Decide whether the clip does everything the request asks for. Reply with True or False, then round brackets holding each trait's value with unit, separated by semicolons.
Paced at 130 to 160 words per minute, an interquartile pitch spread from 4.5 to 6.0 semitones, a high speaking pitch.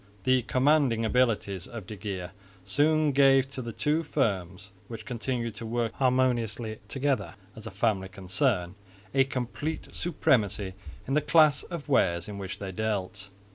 False (150 wpm; 5.2 semitones; 115 Hz)